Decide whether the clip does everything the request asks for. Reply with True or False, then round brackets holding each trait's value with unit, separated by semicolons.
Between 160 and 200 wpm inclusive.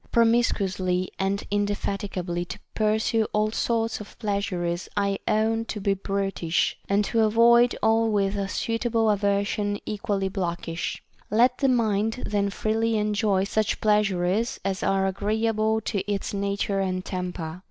False (140 wpm)